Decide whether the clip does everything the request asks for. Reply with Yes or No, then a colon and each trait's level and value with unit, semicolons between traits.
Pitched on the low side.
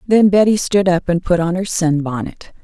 No: medium, 180 Hz